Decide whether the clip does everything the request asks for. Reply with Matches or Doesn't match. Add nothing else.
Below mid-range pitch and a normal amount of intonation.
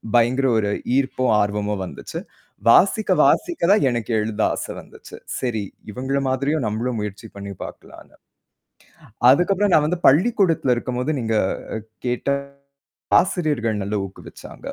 Doesn't match